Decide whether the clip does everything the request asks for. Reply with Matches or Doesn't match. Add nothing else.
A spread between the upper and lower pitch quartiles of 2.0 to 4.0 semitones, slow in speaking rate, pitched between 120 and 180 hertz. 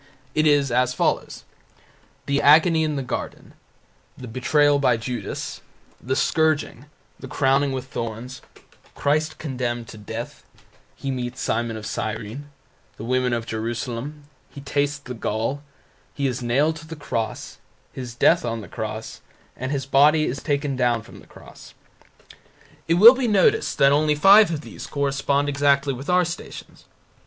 Matches